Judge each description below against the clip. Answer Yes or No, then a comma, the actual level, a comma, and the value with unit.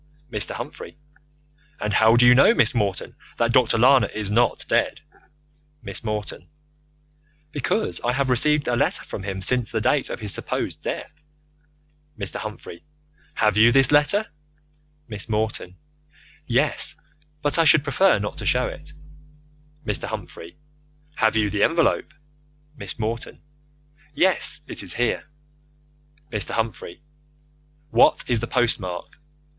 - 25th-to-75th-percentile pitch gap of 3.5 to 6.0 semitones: Yes, average, 4.2 semitones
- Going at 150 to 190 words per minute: No, average, 140 wpm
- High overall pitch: No, low, 115 Hz